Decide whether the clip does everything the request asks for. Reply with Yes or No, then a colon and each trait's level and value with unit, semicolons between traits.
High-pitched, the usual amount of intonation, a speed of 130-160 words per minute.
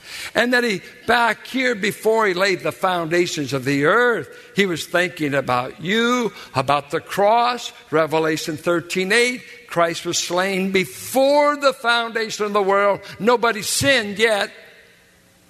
No: high, 200 Hz; wide, 5.7 semitones; slow, 135 wpm